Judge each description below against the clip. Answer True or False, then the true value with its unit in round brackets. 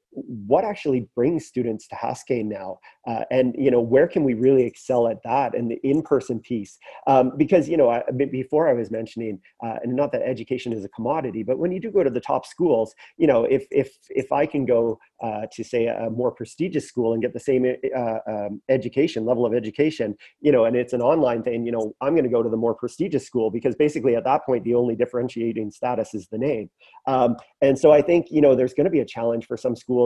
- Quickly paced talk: True (240 wpm)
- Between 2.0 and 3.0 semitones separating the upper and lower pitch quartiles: True (2.6 semitones)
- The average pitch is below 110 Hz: False (125 Hz)